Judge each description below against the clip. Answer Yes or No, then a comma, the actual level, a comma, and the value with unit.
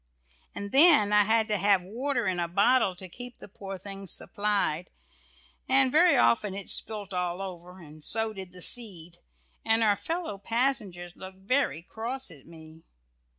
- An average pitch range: Yes, average, 4.2 semitones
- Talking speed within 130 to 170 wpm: Yes, average, 165 wpm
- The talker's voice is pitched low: No, high, 200 Hz